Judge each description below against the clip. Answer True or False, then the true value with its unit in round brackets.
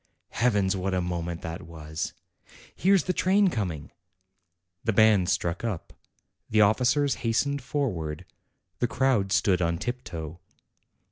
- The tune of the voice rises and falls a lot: True (6.5 semitones)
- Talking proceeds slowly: True (125 wpm)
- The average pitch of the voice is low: True (100 Hz)